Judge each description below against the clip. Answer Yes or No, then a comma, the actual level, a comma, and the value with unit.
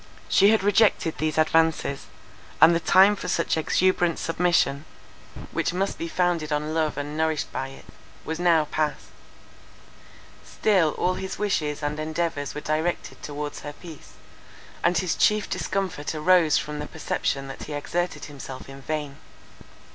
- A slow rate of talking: No, average, 150 wpm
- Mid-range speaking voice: Yes, medium, 160 Hz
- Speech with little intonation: No, average, 3.1 semitones